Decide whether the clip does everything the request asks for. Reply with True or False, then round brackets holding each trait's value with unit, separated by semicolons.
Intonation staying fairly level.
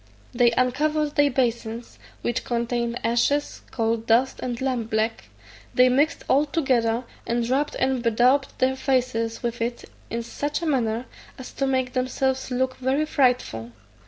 True (2.3 semitones)